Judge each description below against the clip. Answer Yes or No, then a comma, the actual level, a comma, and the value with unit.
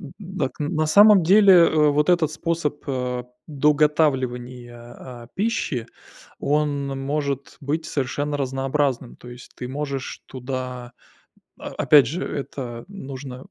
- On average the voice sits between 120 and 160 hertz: Yes, medium, 140 Hz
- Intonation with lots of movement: No, average, 3.2 semitones